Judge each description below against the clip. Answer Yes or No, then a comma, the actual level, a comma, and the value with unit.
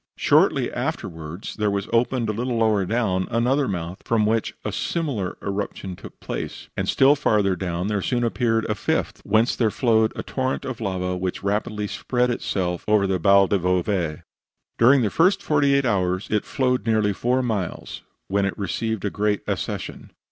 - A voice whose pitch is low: Yes, low, 105 Hz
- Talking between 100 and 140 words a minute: No, average, 175 wpm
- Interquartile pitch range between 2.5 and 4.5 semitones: Yes, average, 3.9 semitones